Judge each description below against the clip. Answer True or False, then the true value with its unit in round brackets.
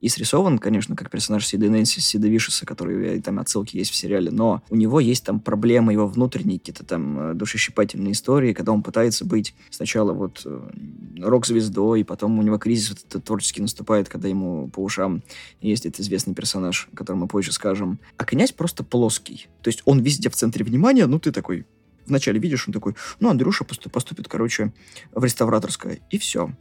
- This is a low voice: True (110 Hz)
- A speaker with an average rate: False (180 wpm)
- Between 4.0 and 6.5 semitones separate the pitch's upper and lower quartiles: False (3.4 semitones)